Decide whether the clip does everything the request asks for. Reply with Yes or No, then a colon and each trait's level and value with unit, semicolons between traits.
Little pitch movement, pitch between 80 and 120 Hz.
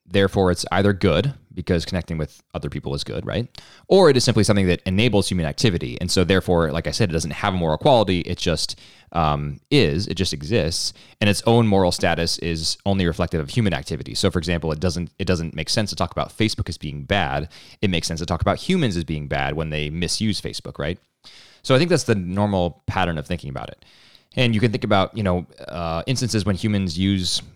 No: average, 3.7 semitones; very low, 90 Hz